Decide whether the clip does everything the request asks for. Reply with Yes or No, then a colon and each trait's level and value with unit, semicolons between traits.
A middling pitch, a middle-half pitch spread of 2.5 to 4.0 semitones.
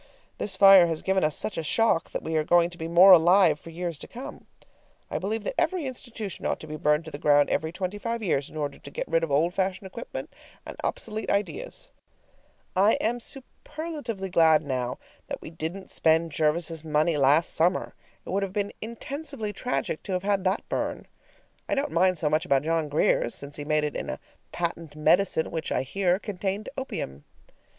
No: medium, 175 Hz; average, 4.5 semitones